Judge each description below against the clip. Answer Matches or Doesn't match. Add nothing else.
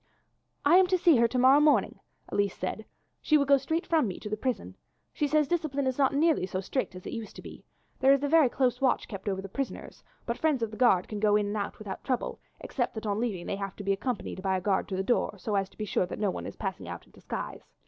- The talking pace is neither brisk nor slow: Doesn't match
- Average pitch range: Doesn't match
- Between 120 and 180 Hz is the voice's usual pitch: Doesn't match